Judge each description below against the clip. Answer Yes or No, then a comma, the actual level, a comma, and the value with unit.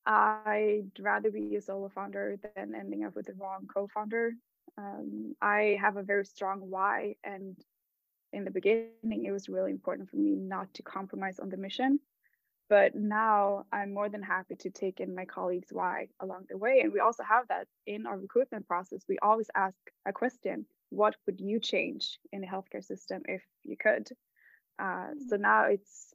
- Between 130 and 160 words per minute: No, average, 185 wpm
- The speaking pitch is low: No, high, 200 Hz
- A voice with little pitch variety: Yes, narrow, 2.1 semitones